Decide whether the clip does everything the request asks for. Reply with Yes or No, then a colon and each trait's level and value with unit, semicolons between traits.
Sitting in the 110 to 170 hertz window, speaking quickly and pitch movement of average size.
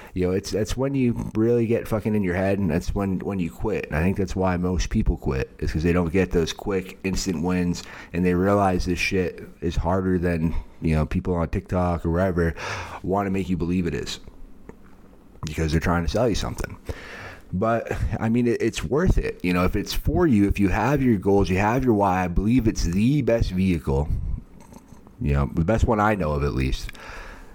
No: very low, 95 Hz; fast, 220 wpm; average, 3.3 semitones